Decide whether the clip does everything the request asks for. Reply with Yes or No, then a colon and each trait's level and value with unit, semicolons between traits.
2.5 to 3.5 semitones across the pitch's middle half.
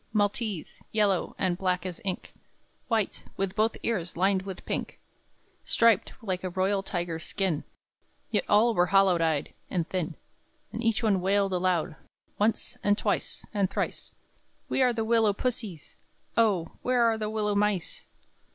Yes: average, 3.2 semitones